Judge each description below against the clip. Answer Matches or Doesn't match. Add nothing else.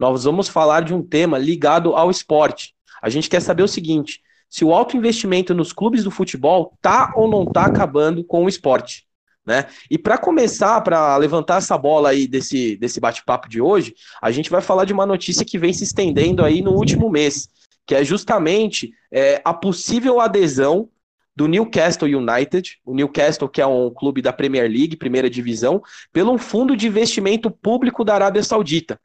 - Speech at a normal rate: Doesn't match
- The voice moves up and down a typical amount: Doesn't match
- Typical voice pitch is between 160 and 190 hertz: Matches